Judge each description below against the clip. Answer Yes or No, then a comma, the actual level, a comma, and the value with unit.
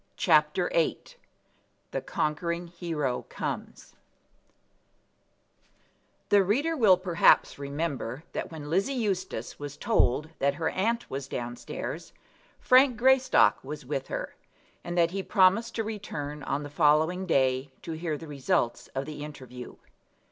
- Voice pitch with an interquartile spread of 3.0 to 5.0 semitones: No, wide, 5.5 semitones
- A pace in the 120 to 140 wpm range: Yes, slow, 135 wpm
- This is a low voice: No, medium, 160 Hz